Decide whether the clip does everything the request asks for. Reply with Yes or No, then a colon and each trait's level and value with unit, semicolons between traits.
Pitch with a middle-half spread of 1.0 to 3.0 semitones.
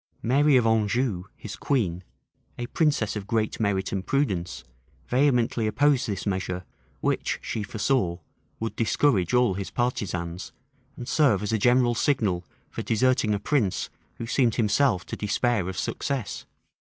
No: average, 4.5 semitones